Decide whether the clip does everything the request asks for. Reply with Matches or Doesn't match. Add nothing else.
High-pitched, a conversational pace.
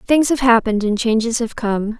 Doesn't match